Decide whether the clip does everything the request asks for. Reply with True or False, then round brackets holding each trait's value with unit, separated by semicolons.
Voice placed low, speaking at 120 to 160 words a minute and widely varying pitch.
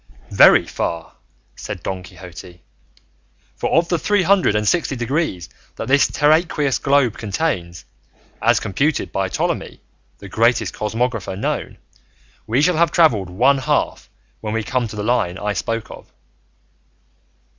True (115 Hz; 140 wpm; 6.9 semitones)